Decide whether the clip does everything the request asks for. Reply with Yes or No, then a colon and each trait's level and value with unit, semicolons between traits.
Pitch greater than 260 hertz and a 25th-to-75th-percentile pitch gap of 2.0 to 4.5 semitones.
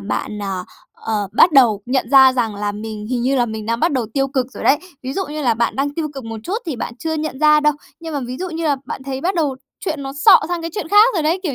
No: very high, 270 Hz; average, 5.2 semitones